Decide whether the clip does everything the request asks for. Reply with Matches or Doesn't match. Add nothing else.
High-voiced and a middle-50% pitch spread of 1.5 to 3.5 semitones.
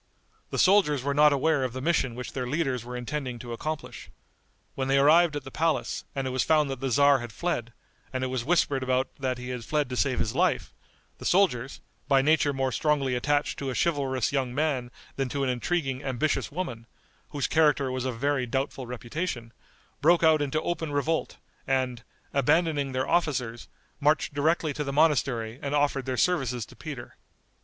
Doesn't match